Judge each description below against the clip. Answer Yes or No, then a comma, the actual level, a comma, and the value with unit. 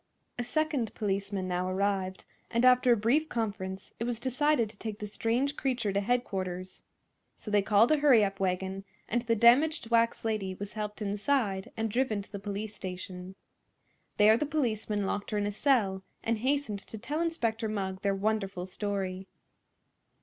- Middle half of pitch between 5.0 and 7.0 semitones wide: No, average, 3.5 semitones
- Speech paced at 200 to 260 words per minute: No, average, 170 wpm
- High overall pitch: Yes, high, 215 Hz